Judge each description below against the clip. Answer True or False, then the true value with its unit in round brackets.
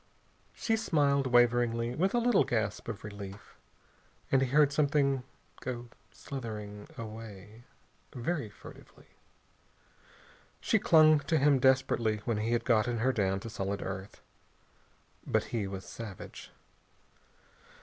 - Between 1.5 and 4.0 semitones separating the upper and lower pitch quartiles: False (4.6 semitones)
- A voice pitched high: False (120 Hz)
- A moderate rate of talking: False (120 wpm)